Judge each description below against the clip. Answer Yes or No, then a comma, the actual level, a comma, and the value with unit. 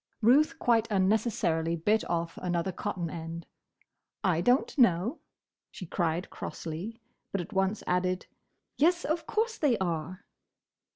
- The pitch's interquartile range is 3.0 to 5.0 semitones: No, wide, 5.5 semitones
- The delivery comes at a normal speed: No, slow, 125 wpm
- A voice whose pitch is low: No, high, 190 Hz